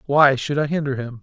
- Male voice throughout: Yes, male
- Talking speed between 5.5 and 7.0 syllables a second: Yes, 5.6 syllables/s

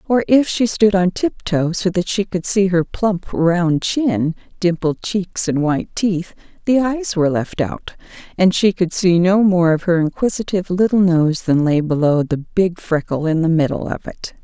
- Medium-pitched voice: Yes, medium, 180 Hz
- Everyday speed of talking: Yes, average, 195 wpm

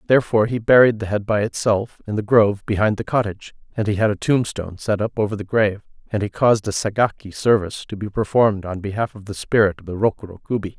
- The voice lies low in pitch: Yes, low, 105 Hz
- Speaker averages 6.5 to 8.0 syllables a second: Yes, 6.6 syllables/s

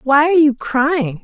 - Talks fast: No, average, 195 wpm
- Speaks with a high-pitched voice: Yes, very high, 280 Hz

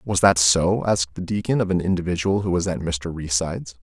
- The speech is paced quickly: Yes, fast, 215 wpm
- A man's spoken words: Yes, male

